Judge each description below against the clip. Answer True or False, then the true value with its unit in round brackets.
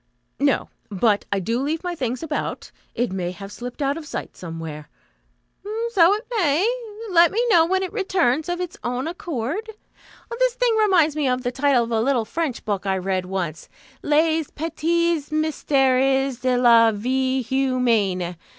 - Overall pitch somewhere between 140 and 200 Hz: False (270 Hz)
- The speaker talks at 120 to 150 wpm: False (165 wpm)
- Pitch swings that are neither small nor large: False (6.4 semitones)